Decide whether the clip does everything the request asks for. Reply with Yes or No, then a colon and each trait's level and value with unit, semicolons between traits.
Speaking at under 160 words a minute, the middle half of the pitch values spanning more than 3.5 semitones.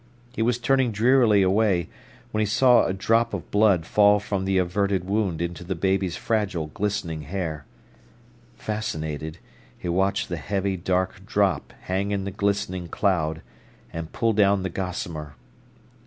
No: average, 150 wpm; average, 3.0 semitones